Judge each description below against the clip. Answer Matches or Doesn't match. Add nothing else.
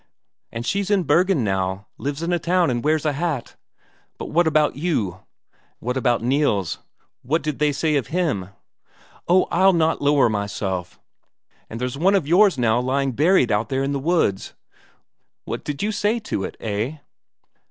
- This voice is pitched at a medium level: Matches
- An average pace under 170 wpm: Doesn't match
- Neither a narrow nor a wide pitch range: Doesn't match